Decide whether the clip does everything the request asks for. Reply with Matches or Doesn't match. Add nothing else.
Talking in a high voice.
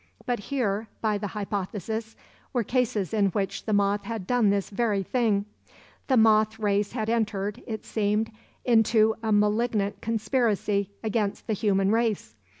Matches